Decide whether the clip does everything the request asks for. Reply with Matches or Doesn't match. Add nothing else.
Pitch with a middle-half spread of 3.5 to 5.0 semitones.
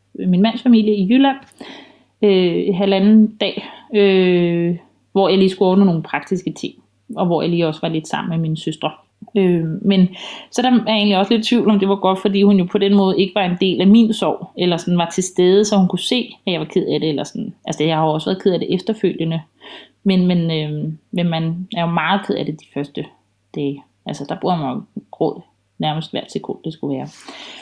Matches